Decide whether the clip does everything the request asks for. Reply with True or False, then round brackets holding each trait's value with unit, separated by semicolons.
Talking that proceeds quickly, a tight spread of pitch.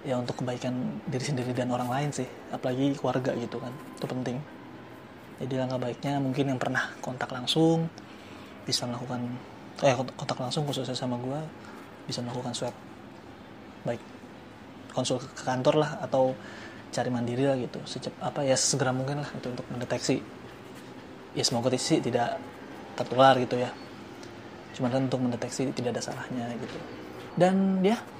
True (150 wpm; 1.9 semitones)